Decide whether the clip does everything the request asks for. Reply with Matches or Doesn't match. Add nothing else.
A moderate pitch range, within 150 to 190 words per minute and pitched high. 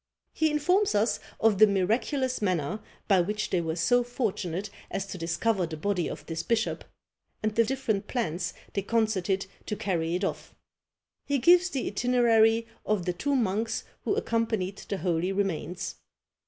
Matches